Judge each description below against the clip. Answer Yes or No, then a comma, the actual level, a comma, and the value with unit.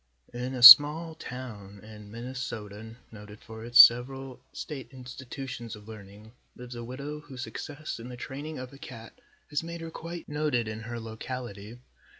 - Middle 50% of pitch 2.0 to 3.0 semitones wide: No, average, 3.7 semitones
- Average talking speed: Yes, average, 160 wpm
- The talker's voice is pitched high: No, low, 125 Hz